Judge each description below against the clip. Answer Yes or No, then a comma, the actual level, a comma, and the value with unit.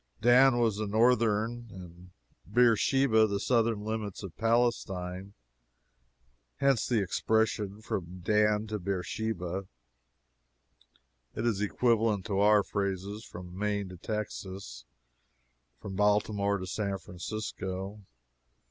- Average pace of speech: No, slow, 105 wpm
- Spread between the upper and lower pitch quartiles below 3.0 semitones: Yes, narrow, 2.6 semitones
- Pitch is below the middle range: Yes, low, 105 Hz